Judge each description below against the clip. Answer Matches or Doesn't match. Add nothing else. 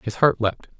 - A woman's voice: Doesn't match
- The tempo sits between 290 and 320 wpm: Doesn't match